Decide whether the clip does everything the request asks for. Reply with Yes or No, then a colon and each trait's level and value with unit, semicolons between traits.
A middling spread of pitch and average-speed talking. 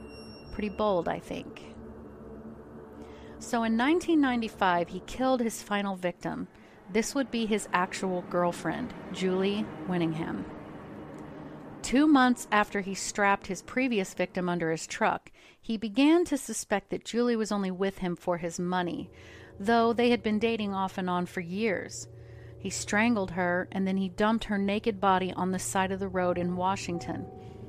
Yes: average, 4.0 semitones; average, 155 wpm